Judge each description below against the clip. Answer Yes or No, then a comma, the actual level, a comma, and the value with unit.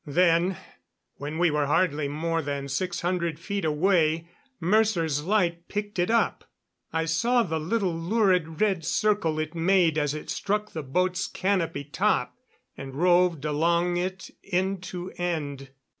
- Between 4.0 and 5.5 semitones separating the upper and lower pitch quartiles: No, average, 3.2 semitones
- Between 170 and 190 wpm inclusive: No, average, 145 wpm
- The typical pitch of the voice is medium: Yes, medium, 170 Hz